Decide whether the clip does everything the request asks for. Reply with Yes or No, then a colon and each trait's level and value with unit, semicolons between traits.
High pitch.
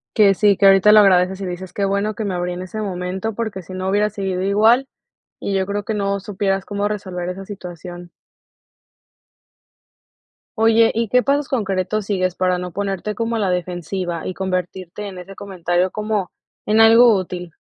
Yes: high, 195 Hz